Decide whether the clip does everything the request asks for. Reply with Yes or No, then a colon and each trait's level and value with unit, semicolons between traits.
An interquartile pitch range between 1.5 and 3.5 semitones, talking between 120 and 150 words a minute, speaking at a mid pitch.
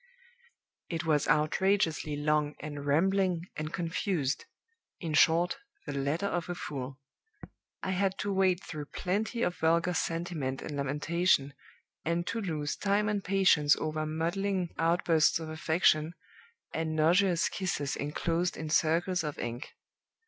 Yes: average, 3.1 semitones; slow, 135 wpm; medium, 165 Hz